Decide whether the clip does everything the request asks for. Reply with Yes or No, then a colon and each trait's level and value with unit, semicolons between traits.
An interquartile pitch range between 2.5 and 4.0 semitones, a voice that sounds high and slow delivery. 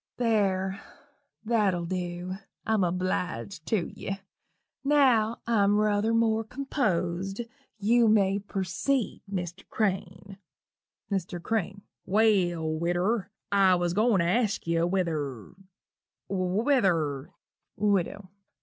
Yes: average, 3.7 semitones; high, 195 Hz; slow, 105 wpm